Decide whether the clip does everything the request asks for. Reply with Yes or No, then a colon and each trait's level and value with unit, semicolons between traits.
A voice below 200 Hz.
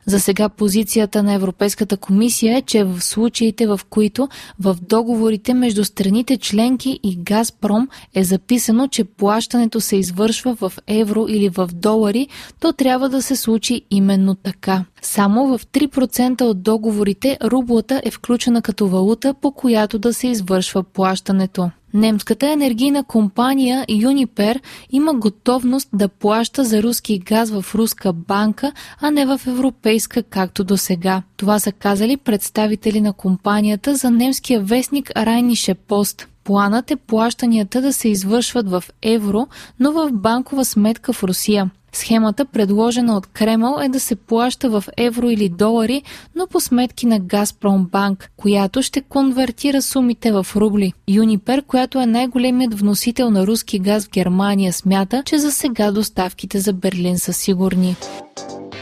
No: high, 220 Hz